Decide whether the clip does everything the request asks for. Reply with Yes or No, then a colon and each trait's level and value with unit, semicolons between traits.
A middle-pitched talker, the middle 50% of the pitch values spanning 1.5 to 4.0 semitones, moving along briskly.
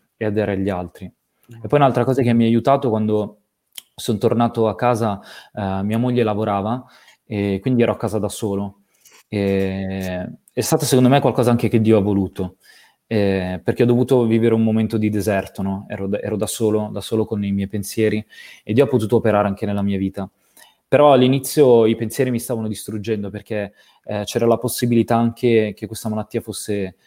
No: low, 110 Hz; narrow, 2.6 semitones; fast, 190 wpm